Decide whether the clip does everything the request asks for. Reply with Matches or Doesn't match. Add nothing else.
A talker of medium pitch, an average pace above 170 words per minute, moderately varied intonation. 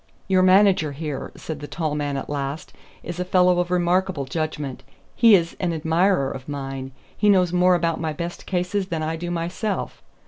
Matches